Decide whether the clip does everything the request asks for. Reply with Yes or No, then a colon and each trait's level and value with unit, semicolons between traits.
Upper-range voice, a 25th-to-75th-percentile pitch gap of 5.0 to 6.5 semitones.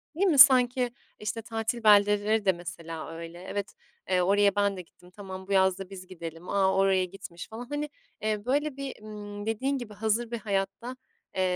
No: high, 205 Hz; average, 3.5 semitones